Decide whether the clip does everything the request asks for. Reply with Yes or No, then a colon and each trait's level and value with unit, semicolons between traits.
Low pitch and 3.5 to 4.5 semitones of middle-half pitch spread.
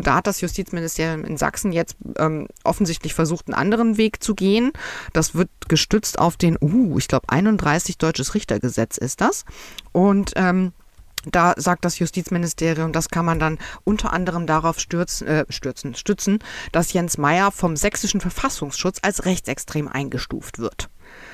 No: medium, 175 Hz; average, 3.9 semitones